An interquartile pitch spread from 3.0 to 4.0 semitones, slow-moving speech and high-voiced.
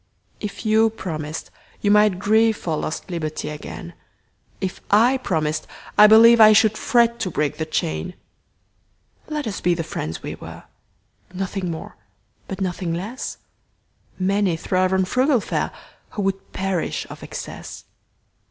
No: average, 4.5 semitones; slow, 120 wpm; high, 195 Hz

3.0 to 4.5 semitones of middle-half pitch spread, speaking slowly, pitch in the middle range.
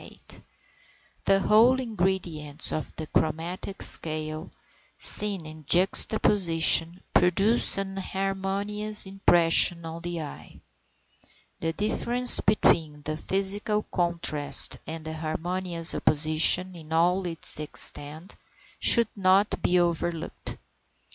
Yes: average, 3.4 semitones; slow, 95 wpm; medium, 175 Hz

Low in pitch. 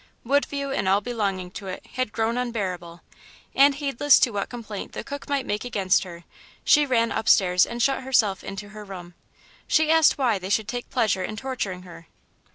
No: high, 220 Hz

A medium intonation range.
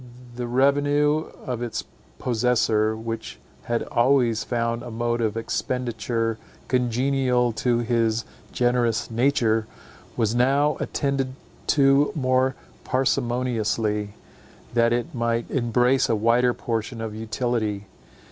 No: narrow, 2.1 semitones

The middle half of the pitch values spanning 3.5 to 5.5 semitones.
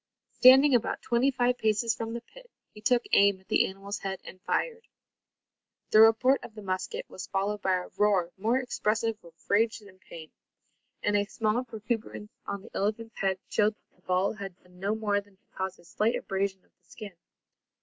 No: average, 2.9 semitones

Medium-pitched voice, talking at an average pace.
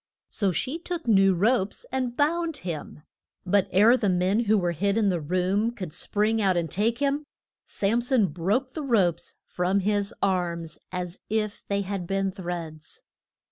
No: high, 200 Hz; average, 170 wpm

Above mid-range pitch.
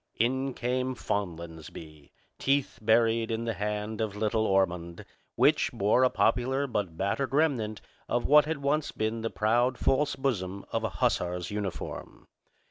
No: low, 110 Hz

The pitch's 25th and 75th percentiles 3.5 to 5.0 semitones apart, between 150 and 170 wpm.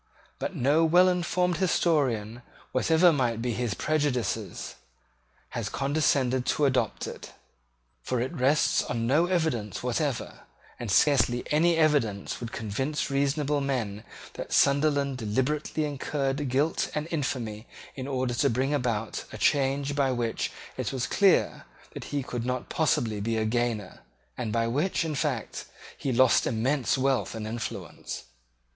No: average, 4.0 semitones; average, 140 wpm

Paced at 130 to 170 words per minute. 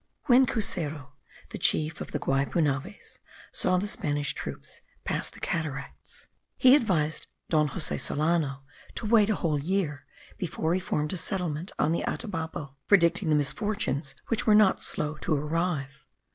Yes: average, 150 wpm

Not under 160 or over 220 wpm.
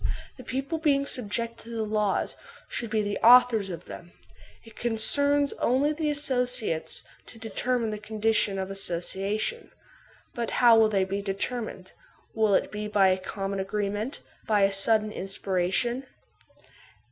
No: average, 145 wpm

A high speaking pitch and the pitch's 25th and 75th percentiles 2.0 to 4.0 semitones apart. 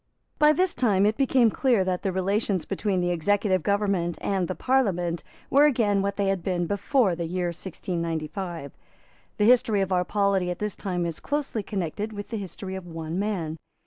Yes: high, 195 Hz; average, 3.0 semitones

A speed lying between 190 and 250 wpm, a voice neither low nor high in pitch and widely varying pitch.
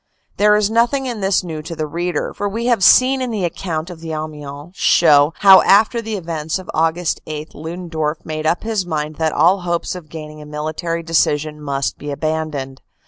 No: average, 195 wpm; medium, 165 Hz; average, 4.0 semitones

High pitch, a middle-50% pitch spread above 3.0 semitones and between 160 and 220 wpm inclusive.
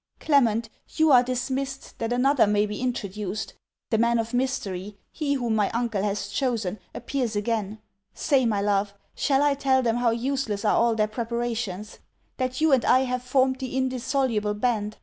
Yes: high, 235 Hz; average, 3.8 semitones; average, 170 wpm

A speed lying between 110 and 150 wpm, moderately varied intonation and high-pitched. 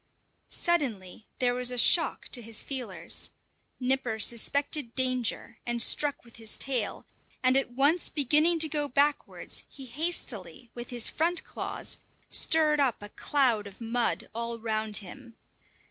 Yes: average, 145 wpm; average, 3.9 semitones; very high, 250 Hz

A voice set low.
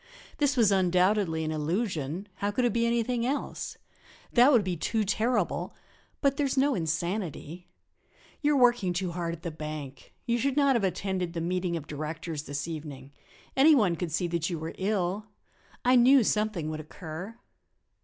No: medium, 185 Hz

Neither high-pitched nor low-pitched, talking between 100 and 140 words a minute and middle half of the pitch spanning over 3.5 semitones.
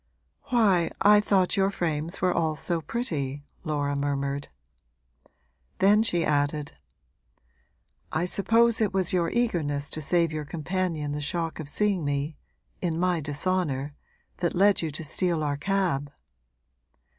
Yes: medium, 165 Hz; slow, 135 wpm; average, 4.4 semitones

